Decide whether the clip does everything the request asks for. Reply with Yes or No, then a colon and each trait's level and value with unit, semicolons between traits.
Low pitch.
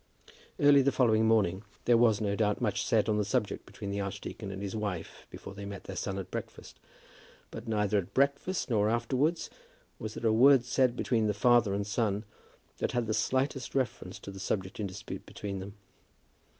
Yes: low, 110 Hz